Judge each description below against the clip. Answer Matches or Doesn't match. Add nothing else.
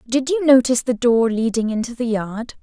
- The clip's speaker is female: Matches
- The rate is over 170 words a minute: Matches